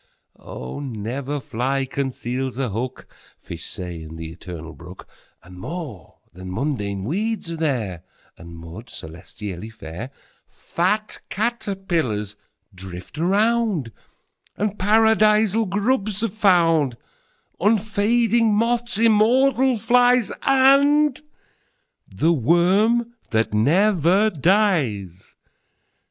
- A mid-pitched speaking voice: Yes, medium, 165 Hz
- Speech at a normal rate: No, slow, 80 wpm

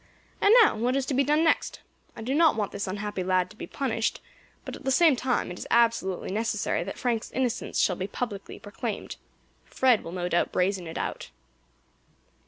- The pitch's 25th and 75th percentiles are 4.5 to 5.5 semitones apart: Yes, average, 5.2 semitones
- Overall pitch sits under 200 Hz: No, high, 220 Hz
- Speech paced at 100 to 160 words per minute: No, average, 195 wpm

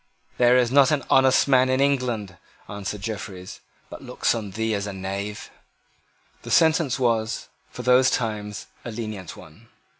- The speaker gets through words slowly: No, average, 155 wpm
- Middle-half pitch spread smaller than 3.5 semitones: No, average, 3.9 semitones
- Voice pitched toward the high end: No, low, 115 Hz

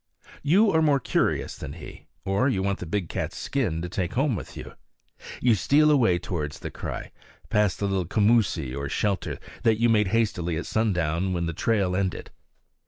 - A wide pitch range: No, average, 4.8 semitones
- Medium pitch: No, low, 100 Hz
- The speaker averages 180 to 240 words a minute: Yes, average, 185 wpm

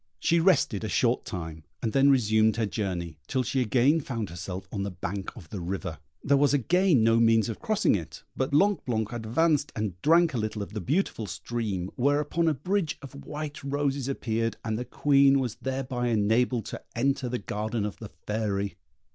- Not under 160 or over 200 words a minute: Yes, average, 190 wpm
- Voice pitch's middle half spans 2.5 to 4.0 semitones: No, average, 5.0 semitones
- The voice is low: Yes, low, 120 Hz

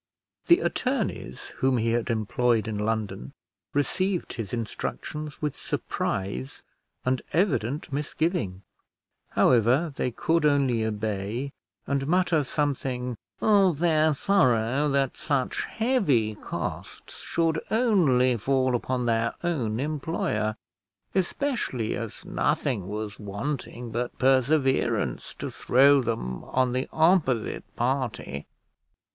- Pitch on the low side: Yes, low, 130 Hz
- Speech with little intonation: No, wide, 5.4 semitones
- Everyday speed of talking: No, slow, 105 wpm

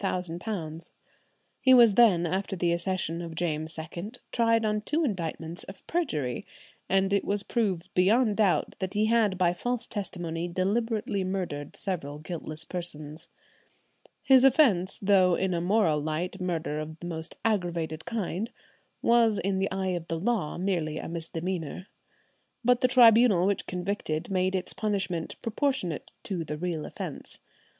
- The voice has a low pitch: No, medium, 185 Hz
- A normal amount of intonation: Yes, average, 4.1 semitones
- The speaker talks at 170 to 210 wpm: No, average, 145 wpm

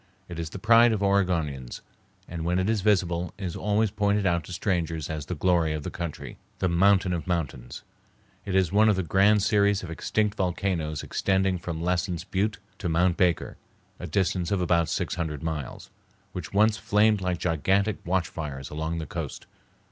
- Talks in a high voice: No, very low, 90 Hz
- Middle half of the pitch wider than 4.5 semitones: No, average, 3.2 semitones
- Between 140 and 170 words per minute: No, average, 185 wpm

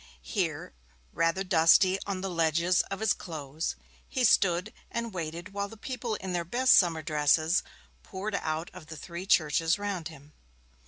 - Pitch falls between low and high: Yes, medium, 175 Hz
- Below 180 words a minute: Yes, average, 160 wpm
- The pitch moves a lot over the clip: No, average, 3.6 semitones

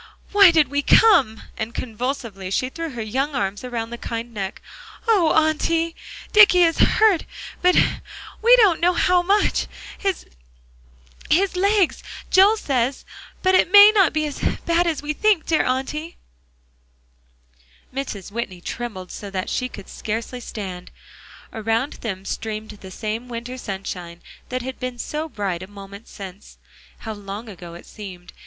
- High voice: Yes, high, 245 Hz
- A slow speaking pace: No, average, 150 wpm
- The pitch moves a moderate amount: No, wide, 8.6 semitones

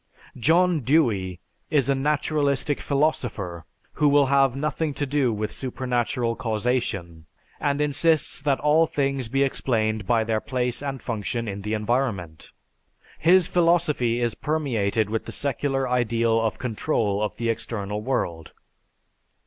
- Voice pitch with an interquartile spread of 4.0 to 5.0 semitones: Yes, average, 4.6 semitones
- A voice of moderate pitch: No, low, 125 Hz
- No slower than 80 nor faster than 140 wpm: Yes, slow, 135 wpm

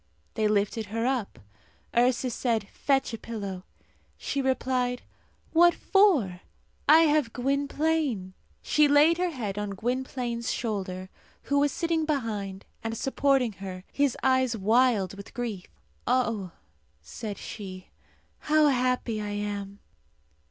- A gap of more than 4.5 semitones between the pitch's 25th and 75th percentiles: Yes, average, 5.1 semitones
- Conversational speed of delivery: No, slow, 125 wpm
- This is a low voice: No, high, 240 Hz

